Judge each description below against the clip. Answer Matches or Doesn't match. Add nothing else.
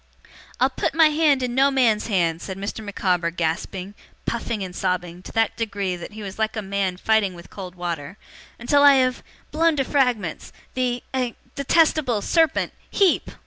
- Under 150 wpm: Doesn't match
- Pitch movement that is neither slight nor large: Doesn't match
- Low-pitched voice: Doesn't match